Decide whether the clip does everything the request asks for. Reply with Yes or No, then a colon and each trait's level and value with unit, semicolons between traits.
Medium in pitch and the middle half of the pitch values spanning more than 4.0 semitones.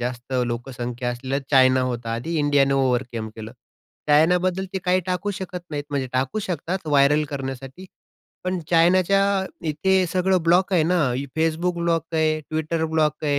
Yes: medium, 155 Hz; average, 5.2 semitones